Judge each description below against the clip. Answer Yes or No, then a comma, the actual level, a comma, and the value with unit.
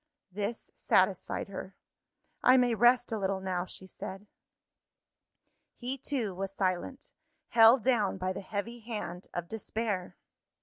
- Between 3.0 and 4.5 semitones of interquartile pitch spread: Yes, average, 4.1 semitones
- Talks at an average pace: No, slow, 130 wpm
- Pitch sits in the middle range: No, high, 210 Hz